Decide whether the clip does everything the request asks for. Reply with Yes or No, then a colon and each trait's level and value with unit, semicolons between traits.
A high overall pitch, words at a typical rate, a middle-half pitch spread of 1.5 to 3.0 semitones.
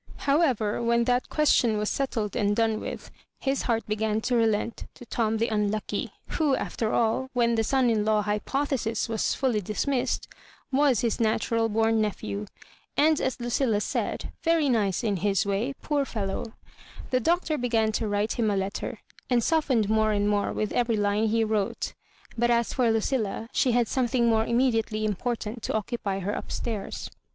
Yes: high, 225 Hz; average, 185 wpm; average, 2.7 semitones